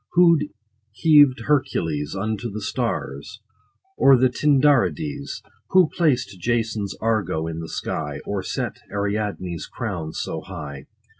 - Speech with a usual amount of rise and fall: No, wide, 7.1 semitones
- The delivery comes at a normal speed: No, slow, 130 wpm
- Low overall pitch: Yes, low, 110 Hz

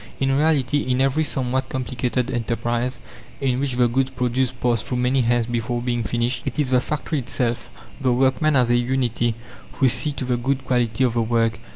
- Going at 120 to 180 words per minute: No, average, 195 wpm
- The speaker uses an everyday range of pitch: No, narrow, 1.8 semitones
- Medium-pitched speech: No, low, 125 Hz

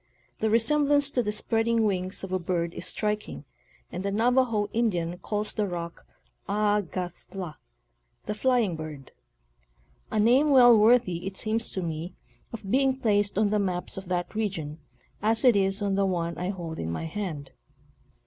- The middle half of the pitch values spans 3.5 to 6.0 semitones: Yes, average, 4.1 semitones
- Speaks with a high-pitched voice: Yes, high, 205 Hz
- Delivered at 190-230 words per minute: No, average, 175 wpm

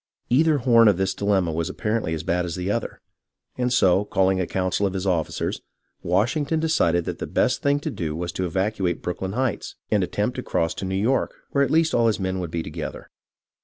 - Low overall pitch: Yes, very low, 95 Hz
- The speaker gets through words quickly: Yes, fast, 220 wpm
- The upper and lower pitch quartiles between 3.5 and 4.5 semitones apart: No, average, 5.0 semitones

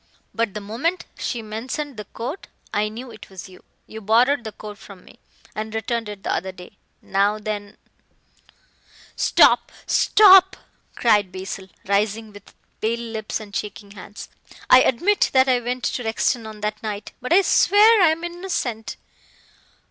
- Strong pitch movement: No, average, 3.6 semitones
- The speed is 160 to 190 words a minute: Yes, average, 165 wpm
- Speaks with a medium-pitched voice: No, high, 220 Hz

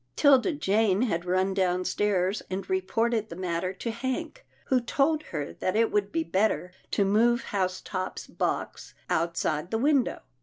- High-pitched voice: Yes, high, 205 Hz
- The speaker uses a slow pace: No, average, 155 wpm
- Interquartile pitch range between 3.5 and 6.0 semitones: Yes, average, 4.5 semitones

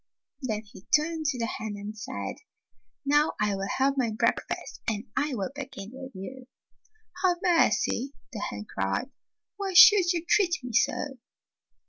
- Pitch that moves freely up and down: Yes, wide, 6.2 semitones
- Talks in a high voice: Yes, very high, 260 Hz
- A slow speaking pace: No, average, 160 wpm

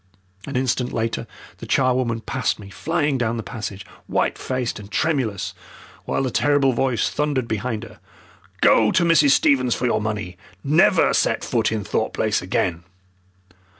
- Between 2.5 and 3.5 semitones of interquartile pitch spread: No, average, 3.9 semitones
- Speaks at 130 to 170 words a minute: Yes, average, 155 wpm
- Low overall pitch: Yes, low, 125 Hz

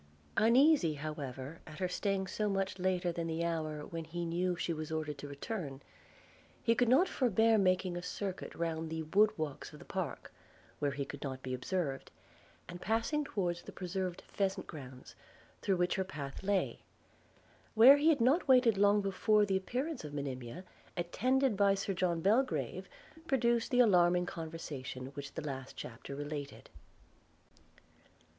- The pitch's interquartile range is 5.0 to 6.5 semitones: Yes, average, 5.3 semitones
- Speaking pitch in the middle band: Yes, medium, 180 Hz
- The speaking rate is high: No, average, 160 wpm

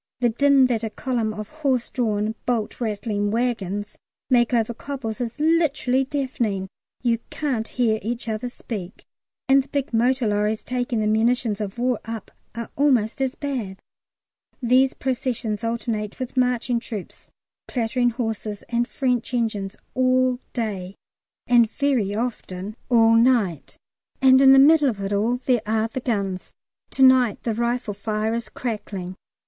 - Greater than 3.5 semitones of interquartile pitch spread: No, average, 3.0 semitones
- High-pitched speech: Yes, high, 235 Hz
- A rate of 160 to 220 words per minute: No, average, 150 wpm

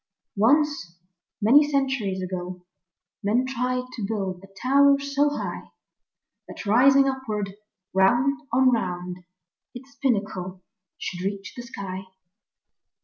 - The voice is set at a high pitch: Yes, high, 225 Hz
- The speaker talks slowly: Yes, slow, 110 wpm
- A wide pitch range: Yes, wide, 5.9 semitones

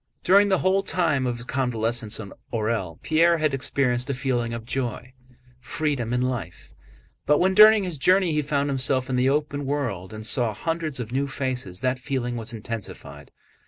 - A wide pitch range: No, average, 4.4 semitones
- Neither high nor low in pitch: No, low, 130 Hz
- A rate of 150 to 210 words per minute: Yes, average, 180 wpm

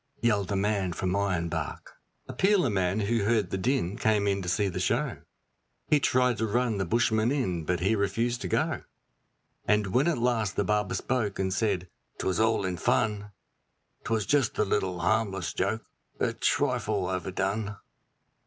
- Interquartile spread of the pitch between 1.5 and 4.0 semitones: Yes, average, 3.3 semitones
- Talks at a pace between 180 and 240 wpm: No, average, 170 wpm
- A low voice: Yes, low, 105 Hz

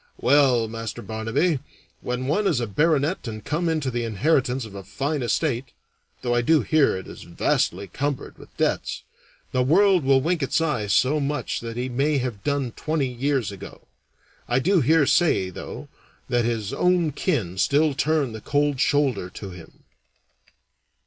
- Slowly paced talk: No, average, 170 wpm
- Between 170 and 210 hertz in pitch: No, low, 135 Hz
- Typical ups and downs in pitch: Yes, average, 4.7 semitones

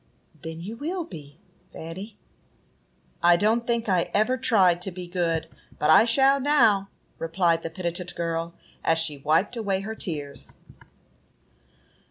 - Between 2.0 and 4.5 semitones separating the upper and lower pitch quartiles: No, average, 5.1 semitones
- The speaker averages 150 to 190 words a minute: No, average, 140 wpm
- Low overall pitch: No, medium, 180 Hz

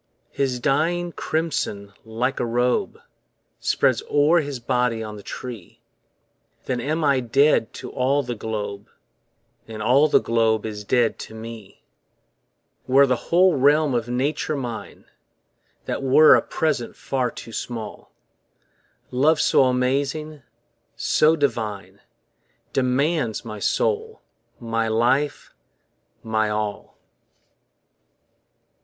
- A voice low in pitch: Yes, low, 125 Hz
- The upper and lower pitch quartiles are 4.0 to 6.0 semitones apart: Yes, average, 4.3 semitones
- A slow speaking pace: Yes, slow, 115 wpm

